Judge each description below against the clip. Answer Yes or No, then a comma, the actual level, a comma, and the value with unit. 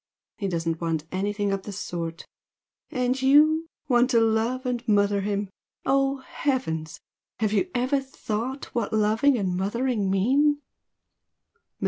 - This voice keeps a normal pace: No, slow, 130 wpm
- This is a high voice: Yes, high, 225 Hz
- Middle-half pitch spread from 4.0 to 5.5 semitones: Yes, average, 5.0 semitones